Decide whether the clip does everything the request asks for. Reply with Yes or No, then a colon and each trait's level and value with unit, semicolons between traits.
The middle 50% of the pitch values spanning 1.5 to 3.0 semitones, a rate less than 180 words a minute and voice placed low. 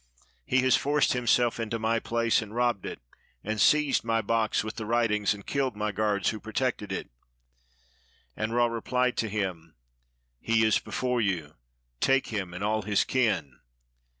Yes: narrow, 2.5 semitones; average, 165 wpm; low, 110 Hz